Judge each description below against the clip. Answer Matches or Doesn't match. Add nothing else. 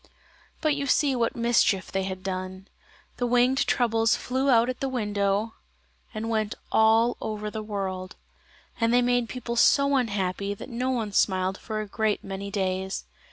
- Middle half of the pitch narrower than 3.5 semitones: Doesn't match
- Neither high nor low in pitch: Doesn't match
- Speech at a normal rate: Matches